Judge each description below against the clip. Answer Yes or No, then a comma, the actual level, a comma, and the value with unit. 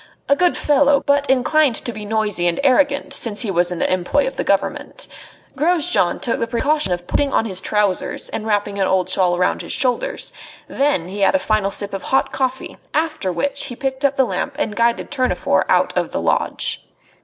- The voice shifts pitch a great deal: Yes, wide, 6.2 semitones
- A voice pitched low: No, high, 240 Hz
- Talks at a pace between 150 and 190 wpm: No, fast, 205 wpm